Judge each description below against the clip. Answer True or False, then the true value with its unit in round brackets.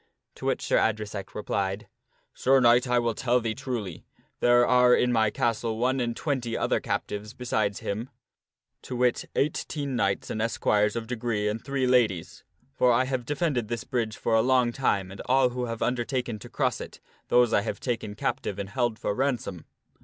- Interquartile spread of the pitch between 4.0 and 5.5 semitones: False (2.8 semitones)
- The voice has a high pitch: False (120 Hz)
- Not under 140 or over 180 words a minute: False (190 wpm)